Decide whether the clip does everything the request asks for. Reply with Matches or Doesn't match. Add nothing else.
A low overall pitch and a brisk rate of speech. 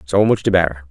Matches